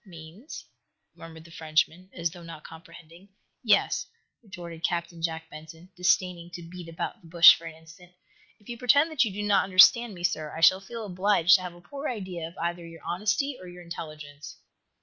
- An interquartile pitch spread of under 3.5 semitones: Yes, average, 2.7 semitones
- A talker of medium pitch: Yes, medium, 175 Hz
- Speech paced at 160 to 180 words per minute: No, average, 190 wpm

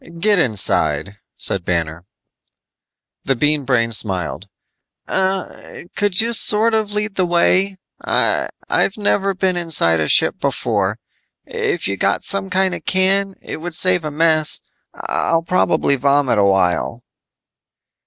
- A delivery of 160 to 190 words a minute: No, slow, 135 wpm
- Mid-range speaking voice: Yes, medium, 165 Hz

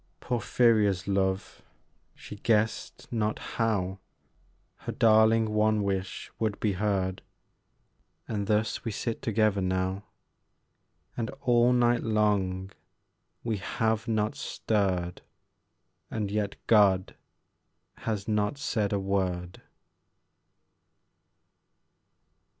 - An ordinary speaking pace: No, slow, 95 wpm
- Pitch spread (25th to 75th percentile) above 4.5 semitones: No, narrow, 2.4 semitones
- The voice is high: No, low, 105 Hz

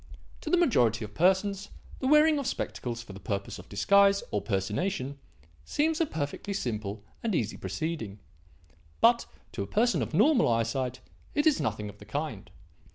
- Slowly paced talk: No, average, 165 wpm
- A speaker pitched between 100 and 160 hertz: Yes, medium, 140 Hz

